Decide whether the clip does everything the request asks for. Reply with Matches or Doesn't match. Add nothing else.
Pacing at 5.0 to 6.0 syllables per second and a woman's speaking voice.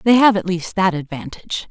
Matches